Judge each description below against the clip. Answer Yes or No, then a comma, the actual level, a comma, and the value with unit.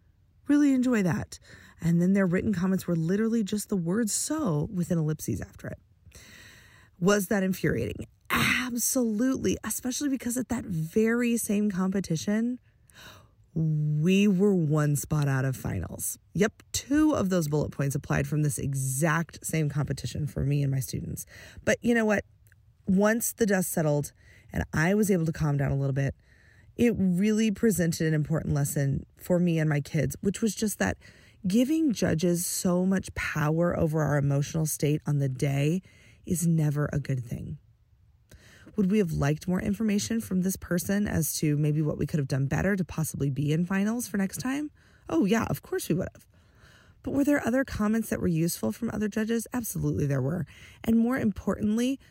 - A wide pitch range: Yes, wide, 6.8 semitones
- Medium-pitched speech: Yes, medium, 170 Hz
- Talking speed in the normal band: Yes, average, 175 wpm